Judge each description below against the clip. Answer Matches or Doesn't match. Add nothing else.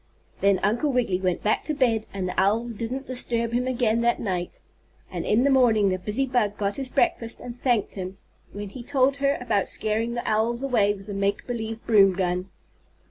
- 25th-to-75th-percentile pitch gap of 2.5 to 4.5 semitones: Matches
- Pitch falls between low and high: Doesn't match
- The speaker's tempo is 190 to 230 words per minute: Matches